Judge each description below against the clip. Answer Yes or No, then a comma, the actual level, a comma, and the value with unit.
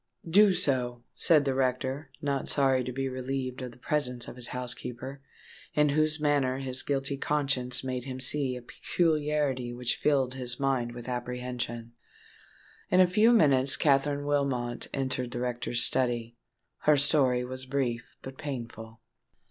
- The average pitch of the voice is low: Yes, low, 130 Hz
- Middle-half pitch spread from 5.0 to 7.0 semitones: No, narrow, 2.4 semitones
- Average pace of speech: Yes, average, 150 wpm